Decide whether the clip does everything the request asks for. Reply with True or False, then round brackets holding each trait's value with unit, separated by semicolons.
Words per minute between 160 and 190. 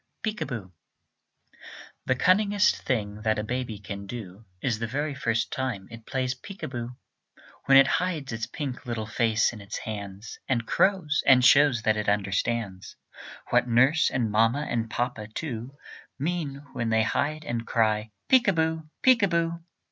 True (170 wpm)